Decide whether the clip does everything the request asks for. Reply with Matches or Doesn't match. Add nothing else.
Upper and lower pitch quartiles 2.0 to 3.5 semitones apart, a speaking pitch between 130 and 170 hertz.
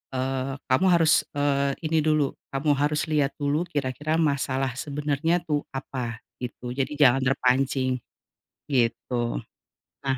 Matches